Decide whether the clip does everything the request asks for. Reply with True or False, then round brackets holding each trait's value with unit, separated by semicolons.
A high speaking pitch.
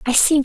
True (275 Hz)